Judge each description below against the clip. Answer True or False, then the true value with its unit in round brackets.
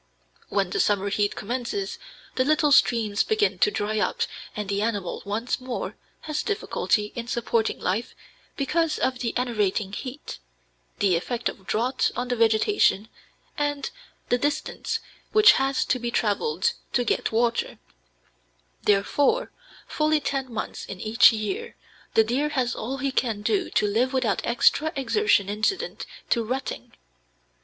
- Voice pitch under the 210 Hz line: False (240 Hz)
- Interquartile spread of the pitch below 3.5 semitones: False (5.0 semitones)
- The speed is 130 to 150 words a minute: True (145 wpm)